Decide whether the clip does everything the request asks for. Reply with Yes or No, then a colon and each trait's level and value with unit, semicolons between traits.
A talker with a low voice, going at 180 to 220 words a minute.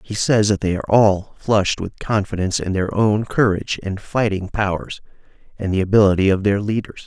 Yes: low, 100 Hz; average, 185 wpm